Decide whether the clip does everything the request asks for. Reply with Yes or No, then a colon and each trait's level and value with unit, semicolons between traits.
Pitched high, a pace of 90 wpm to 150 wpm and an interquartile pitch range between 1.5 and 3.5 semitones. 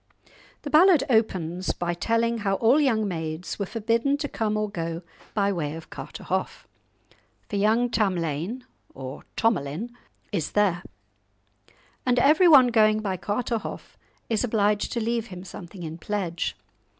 No: high, 210 Hz; average, 140 wpm; average, 4.9 semitones